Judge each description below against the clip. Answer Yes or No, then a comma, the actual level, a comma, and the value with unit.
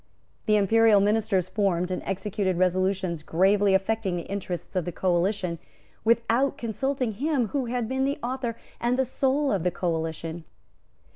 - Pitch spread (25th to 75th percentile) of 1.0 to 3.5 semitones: No, average, 4.4 semitones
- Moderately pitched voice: No, high, 200 Hz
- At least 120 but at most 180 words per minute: Yes, average, 150 wpm